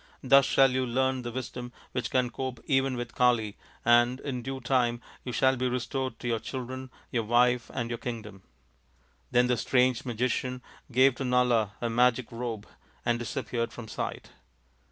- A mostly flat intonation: Yes, narrow, 1.5 semitones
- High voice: No, low, 125 Hz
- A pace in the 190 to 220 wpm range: No, average, 170 wpm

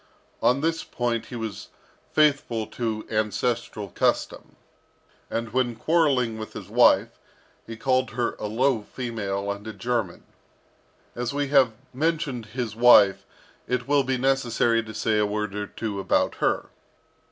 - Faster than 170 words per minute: No, average, 145 wpm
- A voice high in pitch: No, low, 115 Hz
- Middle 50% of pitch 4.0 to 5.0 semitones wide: No, average, 3.1 semitones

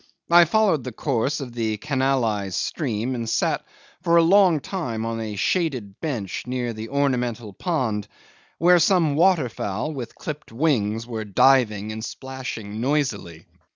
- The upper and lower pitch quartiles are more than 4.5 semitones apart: Yes, wide, 5.6 semitones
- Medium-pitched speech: No, low, 125 Hz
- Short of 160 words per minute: Yes, average, 145 wpm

